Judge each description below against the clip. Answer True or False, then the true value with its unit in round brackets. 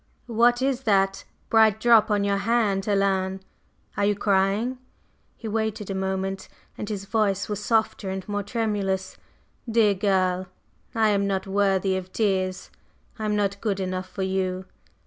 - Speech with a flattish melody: True (2.3 semitones)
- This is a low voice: False (200 Hz)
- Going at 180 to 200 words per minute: False (155 wpm)